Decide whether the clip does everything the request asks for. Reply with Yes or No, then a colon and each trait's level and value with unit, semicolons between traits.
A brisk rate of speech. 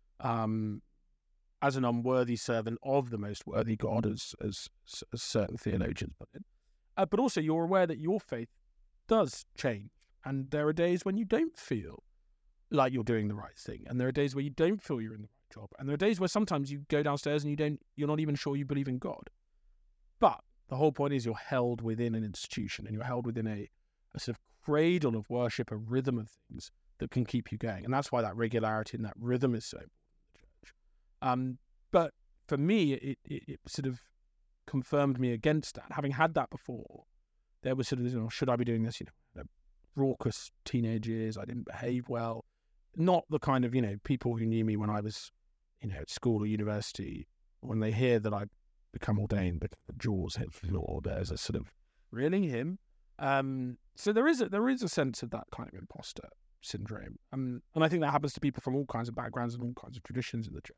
Yes: fast, 220 wpm